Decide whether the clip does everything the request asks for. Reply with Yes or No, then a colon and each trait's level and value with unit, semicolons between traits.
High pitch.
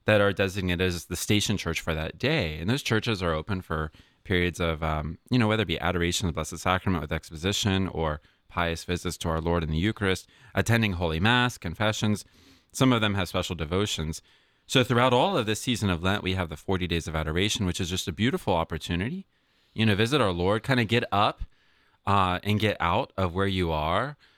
No: very low, 95 Hz